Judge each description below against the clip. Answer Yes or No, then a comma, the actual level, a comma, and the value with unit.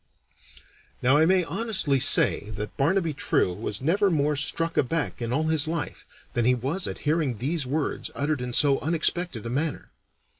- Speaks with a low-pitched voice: No, medium, 145 Hz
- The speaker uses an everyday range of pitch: Yes, average, 4.5 semitones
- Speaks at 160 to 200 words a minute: Yes, average, 175 wpm